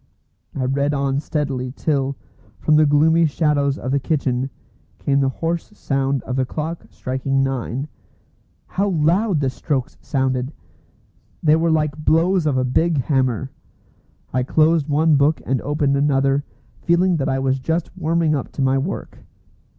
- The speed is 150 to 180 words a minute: Yes, average, 155 wpm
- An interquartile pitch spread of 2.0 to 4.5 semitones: Yes, average, 2.9 semitones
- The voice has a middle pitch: Yes, medium, 145 Hz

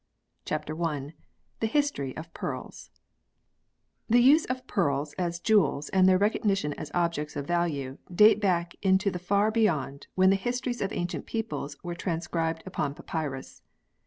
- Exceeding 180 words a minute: No, average, 150 wpm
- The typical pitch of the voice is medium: Yes, medium, 175 Hz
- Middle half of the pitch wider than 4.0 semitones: Yes, average, 5.2 semitones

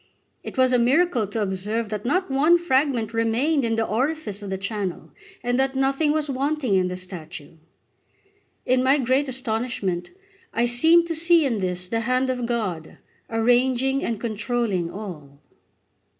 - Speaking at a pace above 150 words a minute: Yes, average, 160 wpm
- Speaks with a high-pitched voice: Yes, high, 240 Hz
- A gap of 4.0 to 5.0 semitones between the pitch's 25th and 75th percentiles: Yes, average, 4.7 semitones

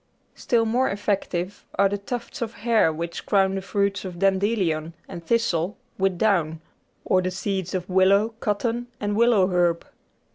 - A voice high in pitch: Yes, high, 195 Hz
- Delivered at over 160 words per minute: No, average, 155 wpm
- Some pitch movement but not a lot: Yes, average, 3.2 semitones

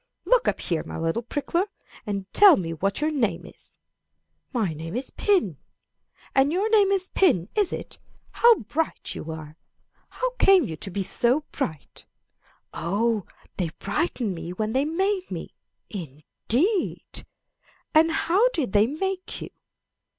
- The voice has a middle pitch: No, very high, 250 Hz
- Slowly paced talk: No, average, 150 wpm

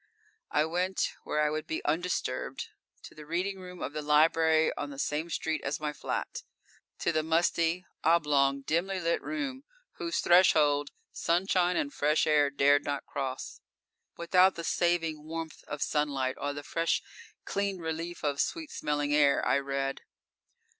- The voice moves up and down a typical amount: Yes, average, 3.1 semitones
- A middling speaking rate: Yes, average, 155 wpm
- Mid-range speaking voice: Yes, medium, 160 Hz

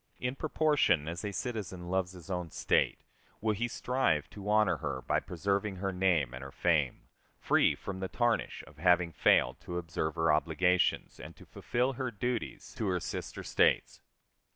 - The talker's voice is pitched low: Yes, very low, 95 Hz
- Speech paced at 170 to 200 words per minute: Yes, average, 175 wpm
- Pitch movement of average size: Yes, average, 4.5 semitones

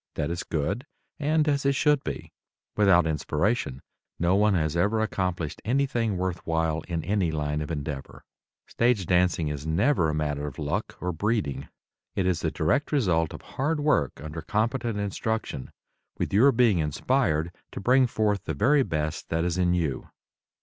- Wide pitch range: Yes, wide, 6.6 semitones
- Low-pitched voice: Yes, very low, 90 Hz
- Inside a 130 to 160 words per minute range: No, average, 170 wpm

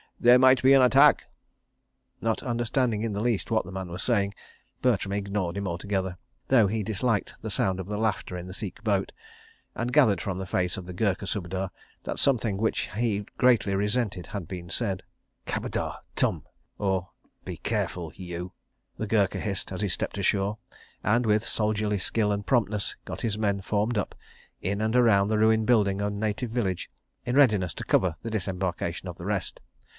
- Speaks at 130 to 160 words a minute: No, average, 175 wpm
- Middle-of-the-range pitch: No, low, 105 Hz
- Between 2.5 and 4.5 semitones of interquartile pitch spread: Yes, average, 2.8 semitones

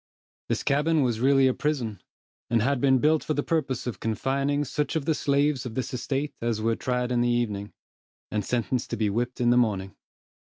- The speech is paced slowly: No, fast, 205 wpm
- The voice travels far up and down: No, average, 3.5 semitones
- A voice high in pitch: No, low, 125 Hz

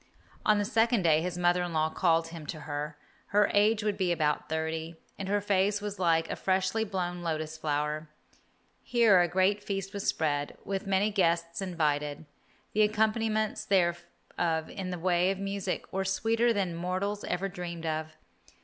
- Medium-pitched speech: Yes, medium, 180 Hz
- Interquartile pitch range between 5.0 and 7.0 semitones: No, average, 3.7 semitones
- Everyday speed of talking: Yes, average, 170 wpm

